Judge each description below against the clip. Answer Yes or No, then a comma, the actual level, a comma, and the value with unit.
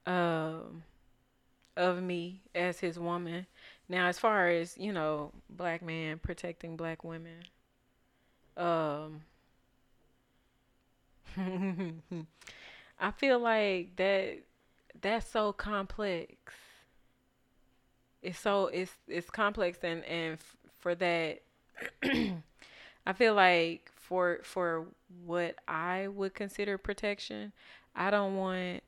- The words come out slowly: Yes, slow, 100 wpm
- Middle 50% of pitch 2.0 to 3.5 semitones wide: Yes, average, 2.7 semitones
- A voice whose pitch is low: No, medium, 180 Hz